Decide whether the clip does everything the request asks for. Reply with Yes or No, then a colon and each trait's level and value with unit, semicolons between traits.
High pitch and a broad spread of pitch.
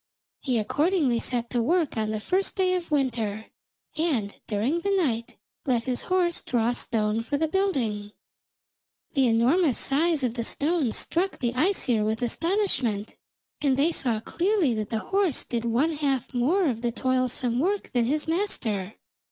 Yes: very high, 260 Hz; wide, 6.5 semitones